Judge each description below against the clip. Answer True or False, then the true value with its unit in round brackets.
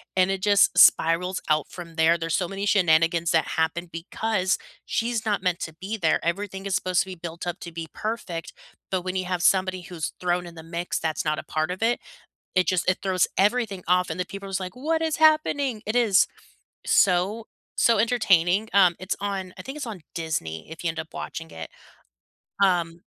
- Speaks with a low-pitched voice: False (185 Hz)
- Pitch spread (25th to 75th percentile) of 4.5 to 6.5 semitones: False (3.3 semitones)